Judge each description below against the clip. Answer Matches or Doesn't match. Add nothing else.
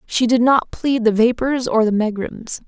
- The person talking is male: Doesn't match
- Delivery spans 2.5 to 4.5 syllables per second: Matches